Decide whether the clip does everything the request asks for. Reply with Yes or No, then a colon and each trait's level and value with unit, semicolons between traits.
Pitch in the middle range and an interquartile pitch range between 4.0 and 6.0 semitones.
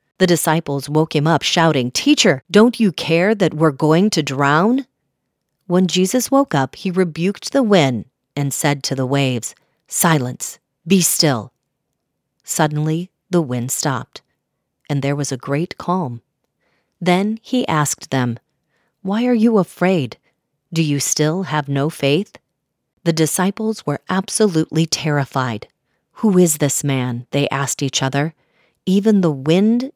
Yes: medium, 160 Hz; average, 5.1 semitones